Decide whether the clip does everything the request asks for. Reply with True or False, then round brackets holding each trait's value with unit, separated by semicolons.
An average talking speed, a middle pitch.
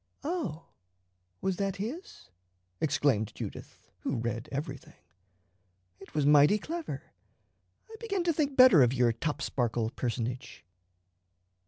False (115 wpm; 150 Hz)